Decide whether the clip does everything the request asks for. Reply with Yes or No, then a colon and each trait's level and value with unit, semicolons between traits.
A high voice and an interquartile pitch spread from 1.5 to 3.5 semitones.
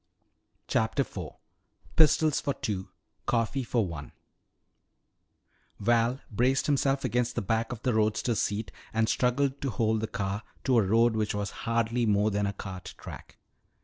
No: low, 115 Hz; average, 3.2 semitones